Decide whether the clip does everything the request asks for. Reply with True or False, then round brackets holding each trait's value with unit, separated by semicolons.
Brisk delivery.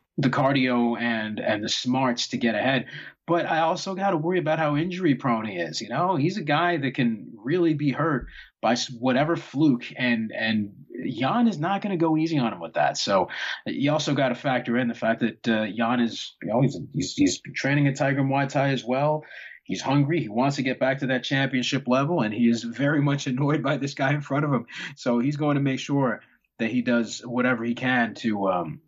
True (230 wpm)